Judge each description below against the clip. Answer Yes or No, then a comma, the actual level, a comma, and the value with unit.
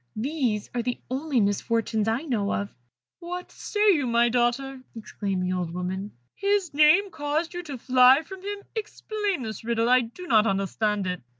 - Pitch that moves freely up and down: Yes, wide, 7.0 semitones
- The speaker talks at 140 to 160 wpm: No, average, 175 wpm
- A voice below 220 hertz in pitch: No, high, 245 Hz